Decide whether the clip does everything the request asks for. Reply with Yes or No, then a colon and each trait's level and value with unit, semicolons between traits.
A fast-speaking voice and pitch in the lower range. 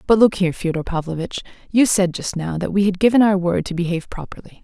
No: fast, 235 wpm; medium, 185 Hz